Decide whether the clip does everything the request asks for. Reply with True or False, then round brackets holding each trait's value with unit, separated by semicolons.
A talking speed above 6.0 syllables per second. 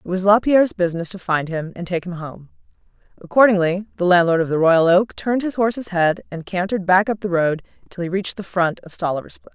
True (6.3 syllables/s)